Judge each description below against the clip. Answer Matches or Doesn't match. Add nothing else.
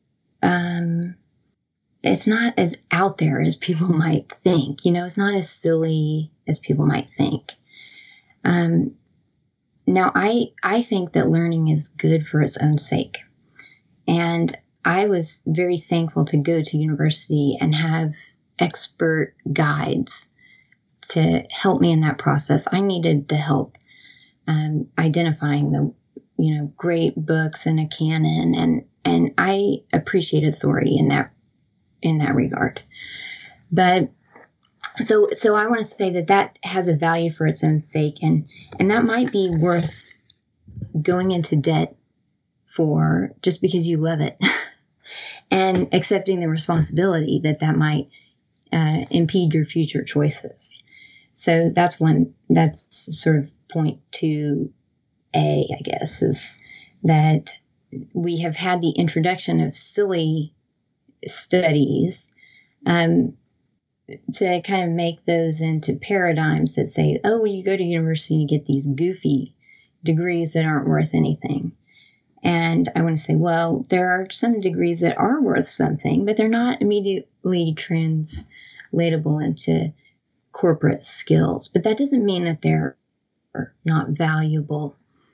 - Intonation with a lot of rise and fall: Doesn't match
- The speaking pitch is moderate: Matches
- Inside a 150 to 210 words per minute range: Doesn't match